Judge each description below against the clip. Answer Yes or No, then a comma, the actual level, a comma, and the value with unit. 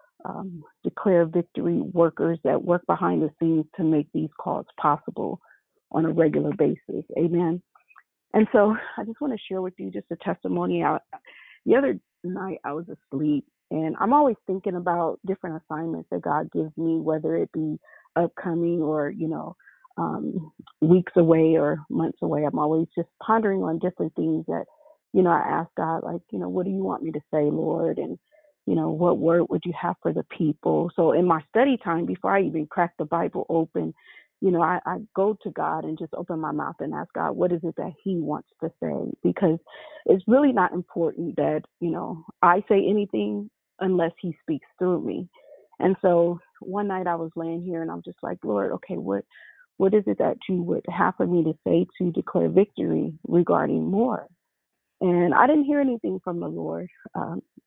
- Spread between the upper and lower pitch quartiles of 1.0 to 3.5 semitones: Yes, average, 3.0 semitones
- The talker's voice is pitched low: No, medium, 175 Hz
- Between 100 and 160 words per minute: No, average, 195 wpm